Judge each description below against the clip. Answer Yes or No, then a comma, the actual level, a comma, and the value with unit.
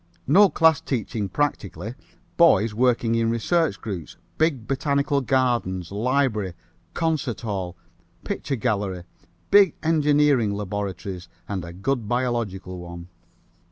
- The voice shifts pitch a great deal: Yes, wide, 6.4 semitones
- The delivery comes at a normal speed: No, slow, 110 wpm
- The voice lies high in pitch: No, low, 115 Hz